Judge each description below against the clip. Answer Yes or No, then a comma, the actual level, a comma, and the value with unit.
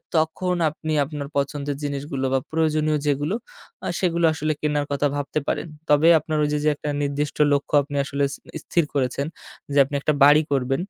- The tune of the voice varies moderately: No, narrow, 1.6 semitones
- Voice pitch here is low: No, medium, 145 Hz